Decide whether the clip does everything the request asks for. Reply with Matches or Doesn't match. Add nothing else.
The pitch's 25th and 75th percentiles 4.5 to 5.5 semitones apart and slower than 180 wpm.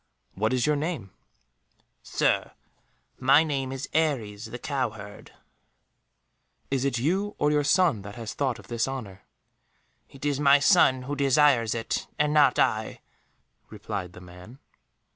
Matches